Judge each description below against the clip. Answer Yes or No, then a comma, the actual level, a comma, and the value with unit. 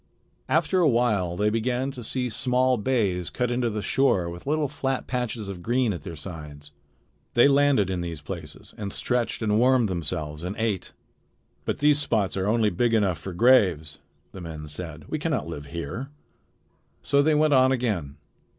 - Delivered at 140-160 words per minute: No, average, 180 wpm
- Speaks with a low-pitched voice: Yes, low, 110 Hz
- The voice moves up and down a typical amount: No, wide, 6.7 semitones